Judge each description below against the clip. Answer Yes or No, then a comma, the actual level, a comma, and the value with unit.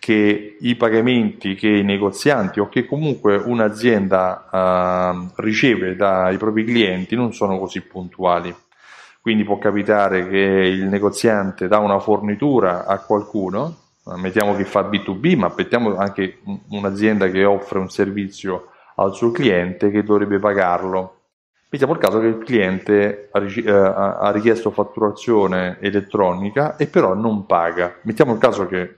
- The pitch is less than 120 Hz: Yes, low, 100 Hz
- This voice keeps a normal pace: Yes, average, 135 wpm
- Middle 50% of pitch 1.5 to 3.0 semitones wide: Yes, narrow, 2.6 semitones